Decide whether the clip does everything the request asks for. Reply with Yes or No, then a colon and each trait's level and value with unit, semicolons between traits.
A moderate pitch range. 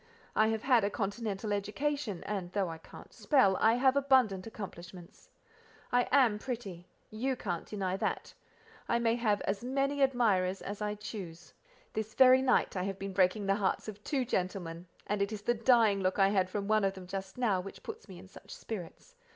Yes: average, 3.9 semitones